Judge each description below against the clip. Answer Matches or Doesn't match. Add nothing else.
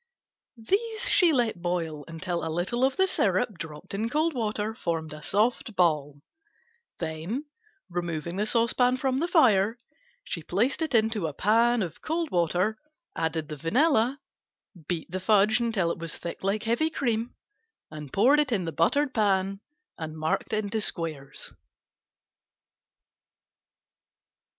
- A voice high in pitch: Matches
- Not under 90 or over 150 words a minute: Matches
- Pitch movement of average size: Doesn't match